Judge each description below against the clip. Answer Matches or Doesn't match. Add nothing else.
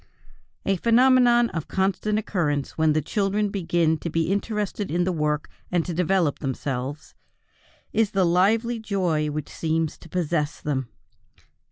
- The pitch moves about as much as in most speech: Matches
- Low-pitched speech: Doesn't match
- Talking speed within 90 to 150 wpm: Matches